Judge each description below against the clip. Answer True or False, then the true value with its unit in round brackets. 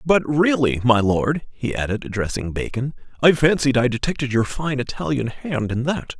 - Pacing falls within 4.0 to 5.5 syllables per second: True (4.9 syllables/s)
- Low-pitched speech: True (130 Hz)